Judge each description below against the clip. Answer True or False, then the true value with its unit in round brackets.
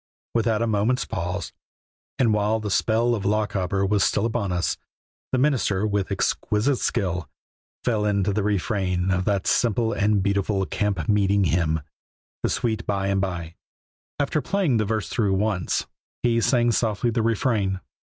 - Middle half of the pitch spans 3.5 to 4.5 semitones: False (2.8 semitones)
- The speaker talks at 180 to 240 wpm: False (155 wpm)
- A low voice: True (105 Hz)